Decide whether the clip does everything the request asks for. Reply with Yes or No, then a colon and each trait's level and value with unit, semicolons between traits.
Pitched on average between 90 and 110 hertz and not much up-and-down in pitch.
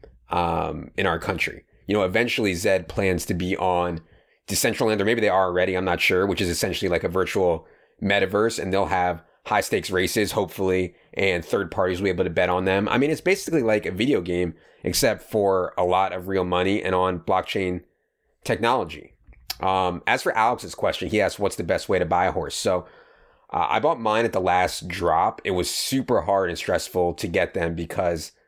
No: very low, 95 Hz; average, 3.2 semitones